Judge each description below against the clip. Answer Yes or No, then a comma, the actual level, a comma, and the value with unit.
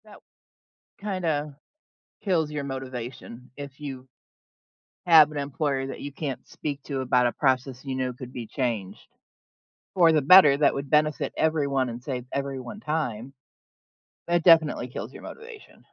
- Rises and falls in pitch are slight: No, average, 3.0 semitones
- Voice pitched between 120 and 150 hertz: Yes, medium, 140 Hz